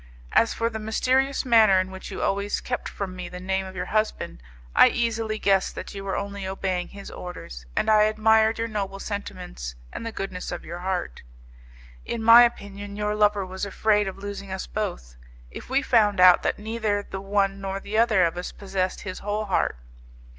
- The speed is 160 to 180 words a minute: No, average, 195 wpm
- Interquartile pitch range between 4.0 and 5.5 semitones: No, narrow, 2.4 semitones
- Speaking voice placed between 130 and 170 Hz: No, high, 200 Hz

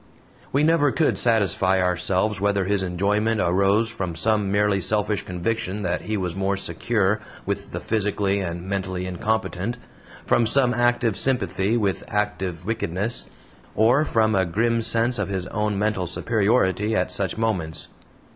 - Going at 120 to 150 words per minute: Yes, average, 145 wpm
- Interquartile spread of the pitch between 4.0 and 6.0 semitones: No, average, 3.1 semitones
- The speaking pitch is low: Yes, low, 105 Hz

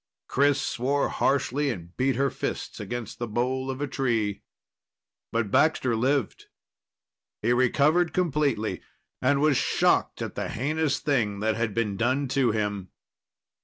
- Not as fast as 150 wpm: Yes, average, 140 wpm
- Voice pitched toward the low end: Yes, low, 130 Hz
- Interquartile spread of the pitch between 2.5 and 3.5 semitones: No, average, 3.9 semitones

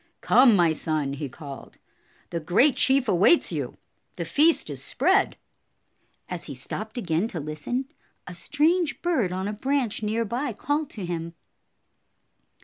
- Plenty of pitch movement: Yes, wide, 8.1 semitones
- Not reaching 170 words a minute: Yes, average, 145 wpm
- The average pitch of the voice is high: Yes, high, 210 Hz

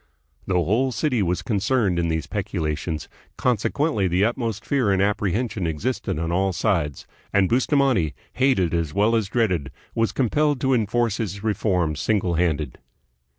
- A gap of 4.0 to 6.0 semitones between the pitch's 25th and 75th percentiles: Yes, wide, 5.5 semitones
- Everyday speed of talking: Yes, average, 150 wpm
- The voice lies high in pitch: No, low, 100 Hz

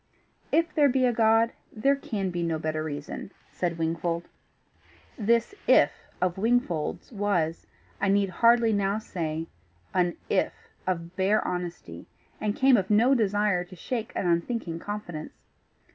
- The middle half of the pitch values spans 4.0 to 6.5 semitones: Yes, average, 4.9 semitones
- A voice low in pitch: No, high, 195 Hz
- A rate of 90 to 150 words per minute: Yes, average, 145 wpm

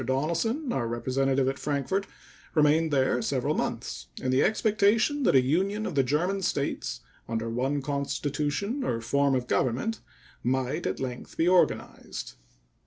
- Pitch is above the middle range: No, medium, 140 Hz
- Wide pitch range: Yes, wide, 6.4 semitones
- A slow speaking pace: No, average, 145 wpm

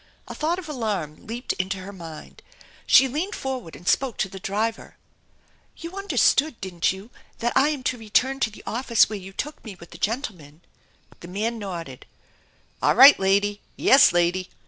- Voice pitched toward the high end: Yes, high, 215 Hz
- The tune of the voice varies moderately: No, wide, 6.1 semitones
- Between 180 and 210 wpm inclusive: Yes, average, 185 wpm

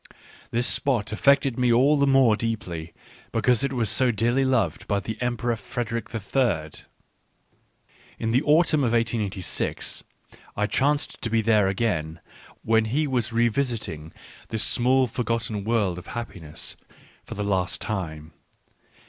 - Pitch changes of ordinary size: Yes, average, 3.6 semitones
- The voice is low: Yes, low, 115 Hz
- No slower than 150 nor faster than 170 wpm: No, average, 140 wpm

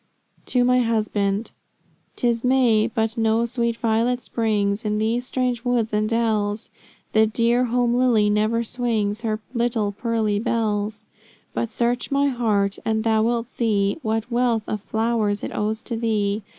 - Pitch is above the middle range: Yes, high, 225 Hz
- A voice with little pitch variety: Yes, narrow, 1.9 semitones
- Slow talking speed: No, average, 150 wpm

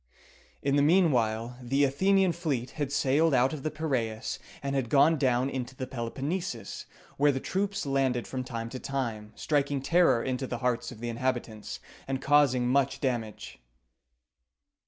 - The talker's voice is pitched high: No, low, 135 Hz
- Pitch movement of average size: Yes, average, 3.1 semitones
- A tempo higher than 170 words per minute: No, average, 160 wpm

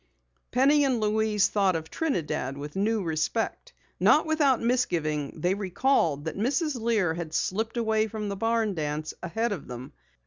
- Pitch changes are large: Yes, wide, 6.4 semitones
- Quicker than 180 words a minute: No, average, 160 wpm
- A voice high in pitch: Yes, high, 210 Hz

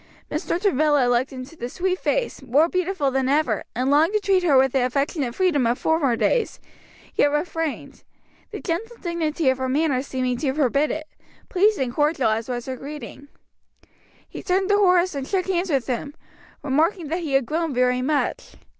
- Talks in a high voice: Yes, very high, 295 Hz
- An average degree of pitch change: Yes, average, 4.9 semitones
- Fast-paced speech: No, average, 185 wpm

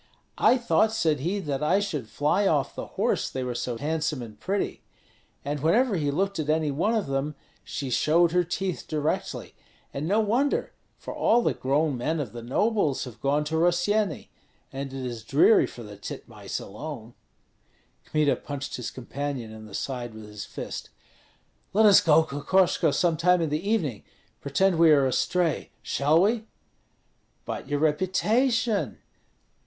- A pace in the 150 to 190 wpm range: Yes, average, 165 wpm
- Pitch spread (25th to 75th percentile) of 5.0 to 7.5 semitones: Yes, wide, 5.6 semitones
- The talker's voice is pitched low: No, medium, 155 Hz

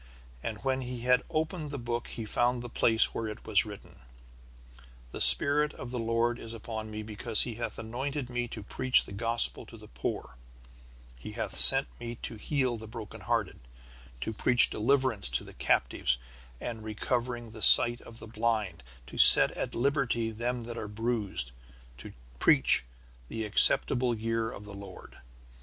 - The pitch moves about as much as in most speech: No, narrow, 2.2 semitones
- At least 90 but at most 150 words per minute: No, average, 170 wpm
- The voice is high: No, low, 115 Hz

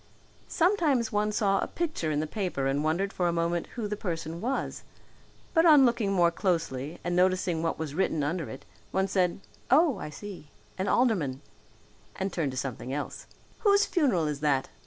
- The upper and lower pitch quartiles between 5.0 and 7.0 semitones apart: Yes, wide, 5.6 semitones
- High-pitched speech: No, medium, 180 Hz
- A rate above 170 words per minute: Yes, average, 180 wpm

